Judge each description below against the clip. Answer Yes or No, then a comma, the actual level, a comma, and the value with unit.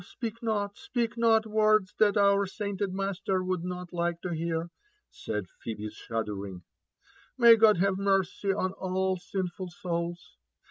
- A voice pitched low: No, high, 190 Hz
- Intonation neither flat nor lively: Yes, average, 3.0 semitones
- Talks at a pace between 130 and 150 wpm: Yes, average, 145 wpm